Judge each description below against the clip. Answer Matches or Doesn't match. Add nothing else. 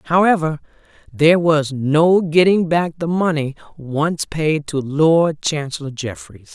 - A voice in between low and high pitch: Matches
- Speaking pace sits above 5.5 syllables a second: Doesn't match